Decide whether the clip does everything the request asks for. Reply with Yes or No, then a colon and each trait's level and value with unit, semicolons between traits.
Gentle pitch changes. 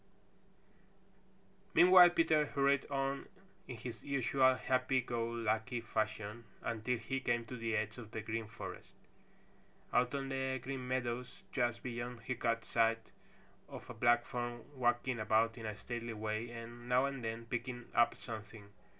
Yes: narrow, 2.2 semitones